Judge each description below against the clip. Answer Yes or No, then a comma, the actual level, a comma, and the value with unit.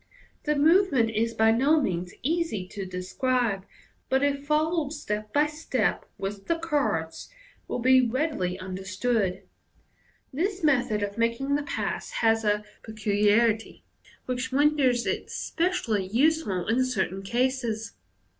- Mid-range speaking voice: No, high, 240 Hz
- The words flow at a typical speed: No, slow, 125 wpm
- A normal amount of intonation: No, wide, 5.7 semitones